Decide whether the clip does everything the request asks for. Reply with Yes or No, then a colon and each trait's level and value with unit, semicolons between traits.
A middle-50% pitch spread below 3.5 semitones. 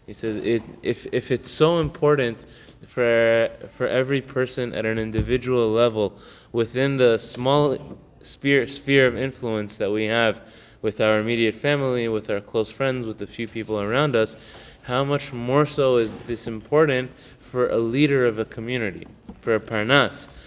Yes: average, 3.0 semitones